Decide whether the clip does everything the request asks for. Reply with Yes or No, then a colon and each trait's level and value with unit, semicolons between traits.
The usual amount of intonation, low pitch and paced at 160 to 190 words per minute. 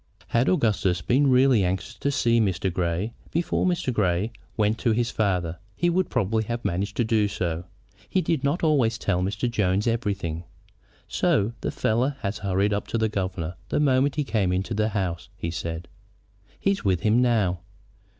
Yes: average, 4.6 semitones; low, 105 Hz; average, 180 wpm